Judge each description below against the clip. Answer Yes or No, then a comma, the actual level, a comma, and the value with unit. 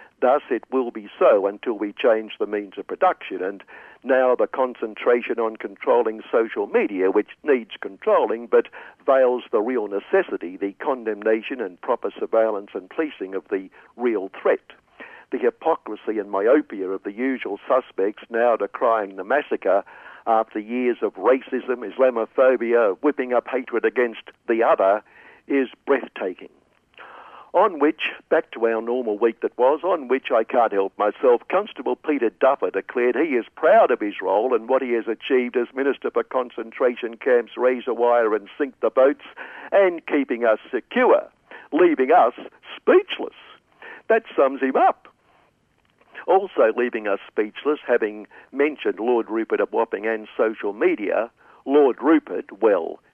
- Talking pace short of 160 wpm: Yes, average, 150 wpm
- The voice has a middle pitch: No, low, 130 Hz